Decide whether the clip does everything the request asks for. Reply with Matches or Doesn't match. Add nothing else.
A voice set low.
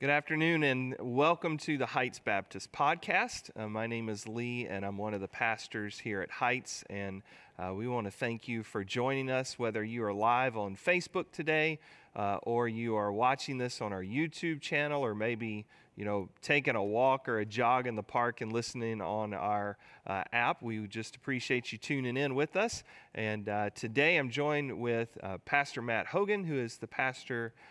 Matches